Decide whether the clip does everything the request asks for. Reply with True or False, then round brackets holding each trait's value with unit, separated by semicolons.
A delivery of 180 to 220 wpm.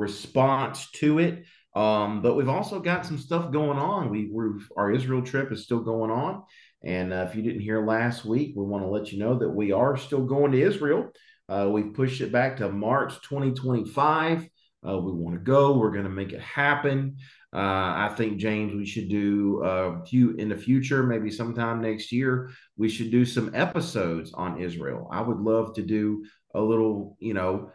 True (200 wpm)